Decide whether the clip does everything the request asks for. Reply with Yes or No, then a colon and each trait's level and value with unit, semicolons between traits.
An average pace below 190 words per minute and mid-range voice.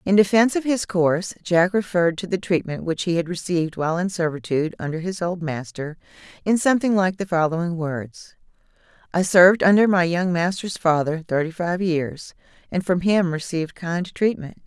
Yes: average, 175 wpm; medium, 175 Hz